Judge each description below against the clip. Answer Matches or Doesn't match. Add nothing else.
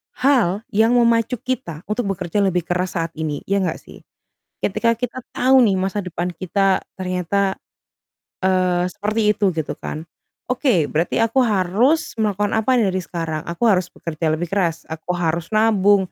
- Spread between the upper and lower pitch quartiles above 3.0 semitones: Matches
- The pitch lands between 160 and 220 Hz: Matches